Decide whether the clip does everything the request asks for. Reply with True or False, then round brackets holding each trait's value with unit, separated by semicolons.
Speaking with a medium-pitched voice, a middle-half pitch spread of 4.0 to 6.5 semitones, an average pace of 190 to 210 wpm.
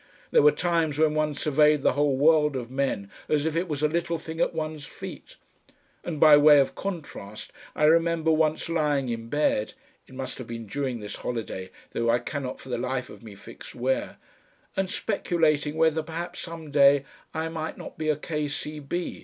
False (150 Hz; 3.3 semitones; 195 wpm)